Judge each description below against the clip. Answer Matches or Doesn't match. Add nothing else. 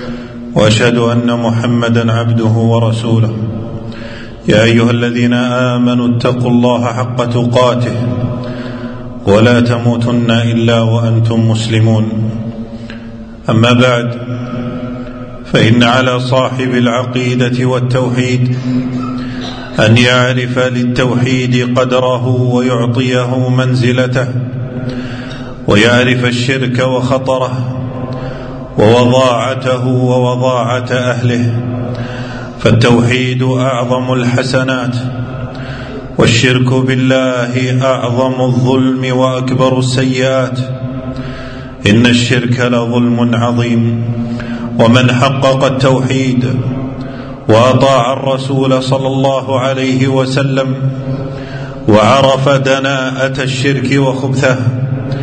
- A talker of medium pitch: Doesn't match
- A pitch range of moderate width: Doesn't match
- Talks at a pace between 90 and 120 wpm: Doesn't match